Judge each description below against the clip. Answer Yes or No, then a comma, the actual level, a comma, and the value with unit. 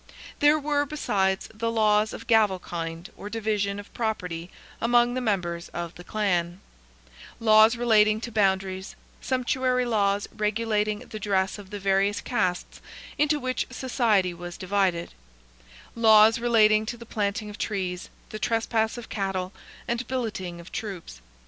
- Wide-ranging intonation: No, average, 3.3 semitones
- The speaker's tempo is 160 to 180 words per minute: No, average, 140 wpm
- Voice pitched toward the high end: Yes, high, 210 Hz